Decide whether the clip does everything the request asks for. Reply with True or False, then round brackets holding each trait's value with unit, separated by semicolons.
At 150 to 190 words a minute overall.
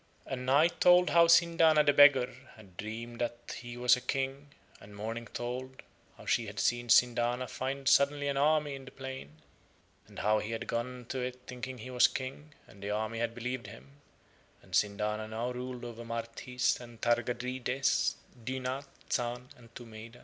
True (170 wpm)